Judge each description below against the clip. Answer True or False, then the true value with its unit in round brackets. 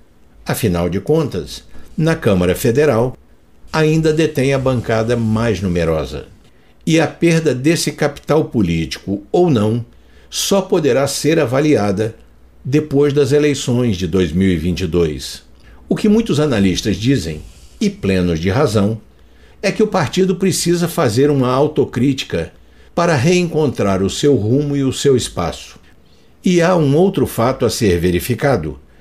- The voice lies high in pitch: False (120 Hz)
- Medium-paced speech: True (130 wpm)